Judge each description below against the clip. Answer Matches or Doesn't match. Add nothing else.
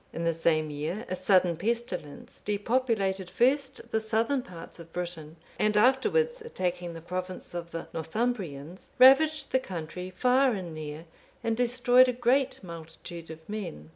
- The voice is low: Doesn't match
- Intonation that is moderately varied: Doesn't match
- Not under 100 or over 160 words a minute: Matches